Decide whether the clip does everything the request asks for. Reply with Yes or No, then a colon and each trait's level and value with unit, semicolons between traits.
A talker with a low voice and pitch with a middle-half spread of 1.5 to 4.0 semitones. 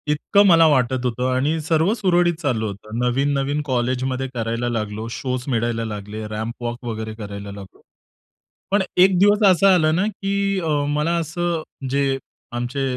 No: low, 130 Hz; wide, 6.2 semitones